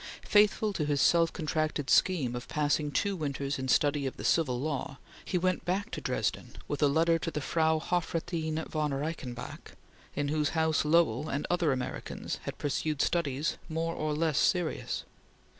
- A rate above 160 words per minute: Yes, average, 170 wpm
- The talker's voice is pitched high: No, medium, 155 Hz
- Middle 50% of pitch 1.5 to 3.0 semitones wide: Yes, narrow, 2.5 semitones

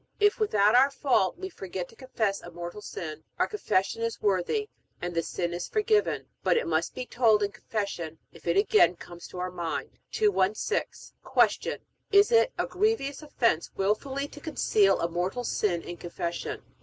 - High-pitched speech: Yes, high, 210 Hz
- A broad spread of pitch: Yes, wide, 8.3 semitones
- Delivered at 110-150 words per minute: No, average, 175 wpm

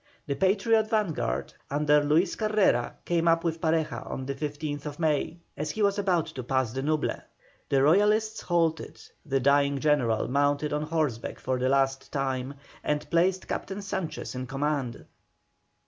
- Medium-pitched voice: Yes, medium, 150 Hz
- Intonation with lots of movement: No, average, 3.8 semitones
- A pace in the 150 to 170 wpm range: Yes, average, 155 wpm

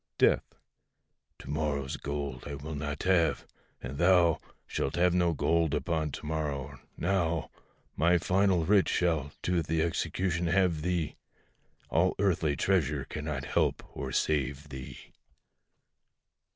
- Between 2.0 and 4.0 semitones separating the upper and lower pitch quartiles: Yes, average, 3.3 semitones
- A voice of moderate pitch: No, very low, 80 Hz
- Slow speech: Yes, slow, 125 wpm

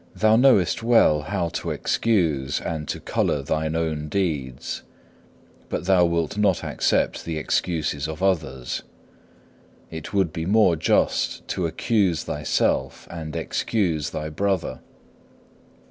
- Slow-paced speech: Yes, slow, 130 wpm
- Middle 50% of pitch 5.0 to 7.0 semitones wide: No, average, 4.1 semitones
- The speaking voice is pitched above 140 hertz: No, very low, 85 Hz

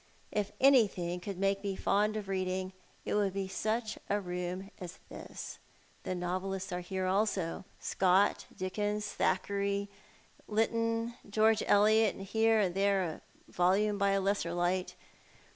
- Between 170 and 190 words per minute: No, average, 145 wpm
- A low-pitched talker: No, high, 195 Hz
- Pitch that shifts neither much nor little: No, narrow, 2.2 semitones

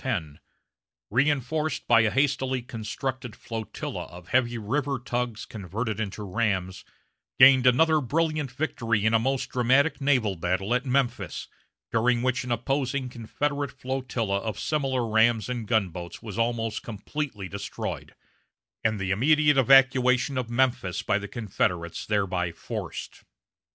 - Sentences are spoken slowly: Yes, slow, 130 wpm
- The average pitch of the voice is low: Yes, low, 120 Hz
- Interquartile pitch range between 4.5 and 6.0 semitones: No, average, 3.9 semitones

